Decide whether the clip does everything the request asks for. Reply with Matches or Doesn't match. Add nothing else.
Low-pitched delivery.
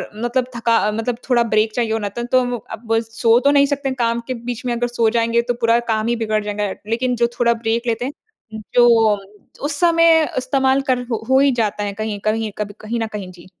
Doesn't match